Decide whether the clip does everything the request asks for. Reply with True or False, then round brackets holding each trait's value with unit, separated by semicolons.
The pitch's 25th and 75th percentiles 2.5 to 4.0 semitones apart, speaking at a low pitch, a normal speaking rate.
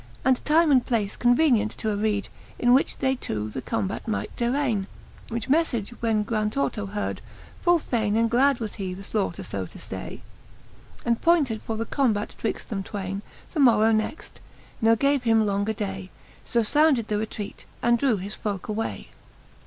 False (3.3 semitones; 225 Hz; 170 wpm)